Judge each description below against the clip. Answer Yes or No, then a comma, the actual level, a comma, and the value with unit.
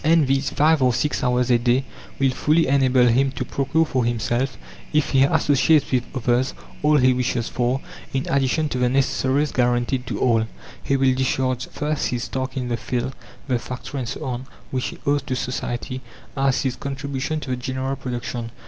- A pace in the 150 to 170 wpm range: No, average, 190 wpm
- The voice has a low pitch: Yes, low, 130 Hz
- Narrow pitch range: Yes, narrow, 1.8 semitones